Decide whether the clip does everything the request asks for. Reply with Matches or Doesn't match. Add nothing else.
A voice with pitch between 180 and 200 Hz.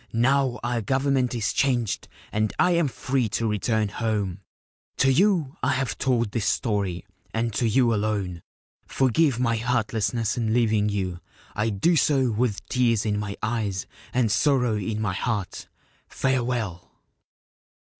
Doesn't match